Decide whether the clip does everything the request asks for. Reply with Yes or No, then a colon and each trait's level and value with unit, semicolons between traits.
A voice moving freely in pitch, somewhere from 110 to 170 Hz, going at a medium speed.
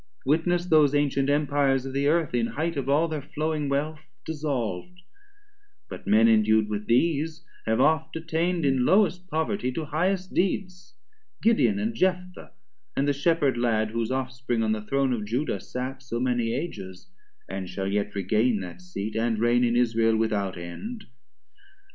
Yes: wide, 6.1 semitones; low, 135 Hz; average, 165 wpm